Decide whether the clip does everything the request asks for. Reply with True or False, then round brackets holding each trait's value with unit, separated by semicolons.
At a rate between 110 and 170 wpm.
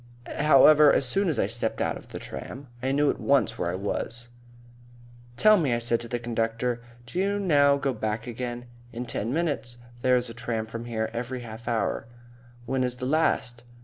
False (195 wpm)